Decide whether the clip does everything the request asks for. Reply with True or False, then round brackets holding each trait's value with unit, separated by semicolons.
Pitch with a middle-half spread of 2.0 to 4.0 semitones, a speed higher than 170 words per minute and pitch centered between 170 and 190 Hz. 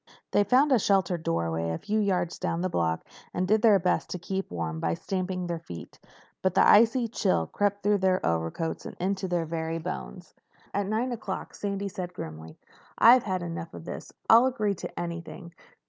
True (3.7 semitones; 190 wpm; 185 Hz)